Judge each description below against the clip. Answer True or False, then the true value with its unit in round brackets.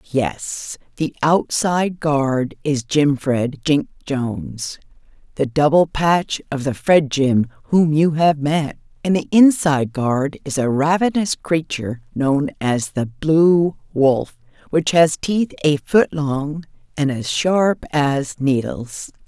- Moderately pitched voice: True (145 Hz)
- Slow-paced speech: True (130 wpm)